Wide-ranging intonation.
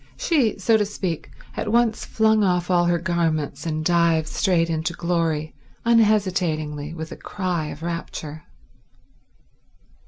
No: average, 3.9 semitones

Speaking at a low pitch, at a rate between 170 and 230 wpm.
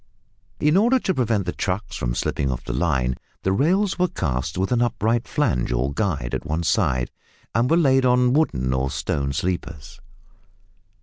Yes: very low, 95 Hz; average, 175 wpm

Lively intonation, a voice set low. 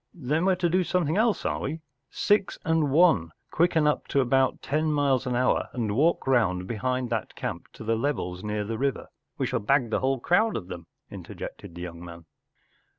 Yes: wide, 7.0 semitones; low, 130 Hz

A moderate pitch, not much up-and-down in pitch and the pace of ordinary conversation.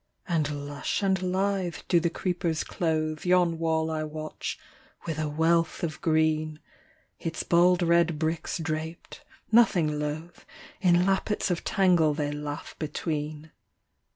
No: medium, 160 Hz; narrow, 2.2 semitones; slow, 130 wpm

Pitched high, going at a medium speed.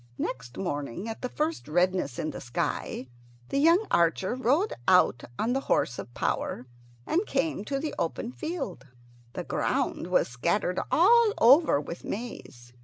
Yes: high, 205 Hz; average, 155 wpm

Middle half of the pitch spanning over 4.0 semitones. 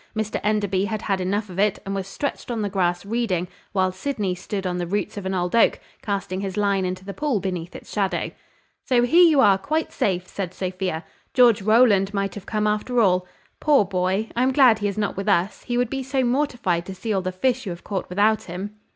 No: average, 3.4 semitones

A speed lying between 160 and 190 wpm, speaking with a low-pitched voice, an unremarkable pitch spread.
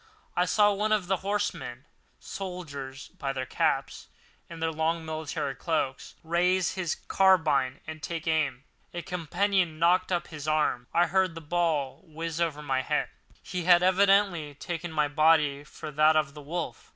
No: average, 165 wpm; medium, 165 Hz; average, 3.3 semitones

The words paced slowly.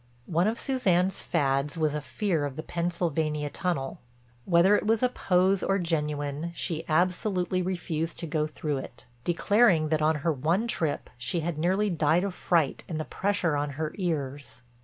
No: average, 175 wpm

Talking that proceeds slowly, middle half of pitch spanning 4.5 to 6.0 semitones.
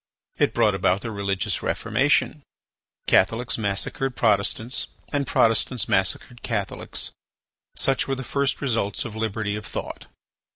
No: slow, 125 wpm; average, 3.6 semitones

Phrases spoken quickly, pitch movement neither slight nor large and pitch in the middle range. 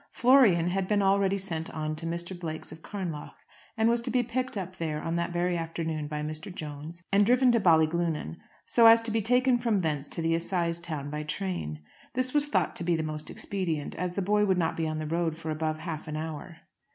Yes: fast, 225 wpm; average, 4.1 semitones; medium, 170 Hz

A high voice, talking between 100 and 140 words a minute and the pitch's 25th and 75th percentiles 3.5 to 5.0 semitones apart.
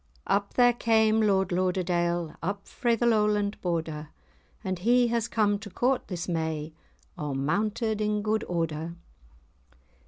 Yes: high, 200 Hz; slow, 135 wpm; average, 4.2 semitones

